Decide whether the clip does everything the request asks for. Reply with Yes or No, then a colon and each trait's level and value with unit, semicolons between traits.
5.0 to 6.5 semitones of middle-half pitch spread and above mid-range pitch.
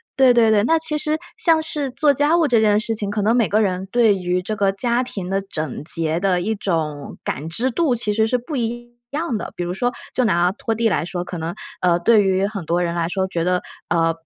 Yes: average, 5.3 semitones; high, 205 Hz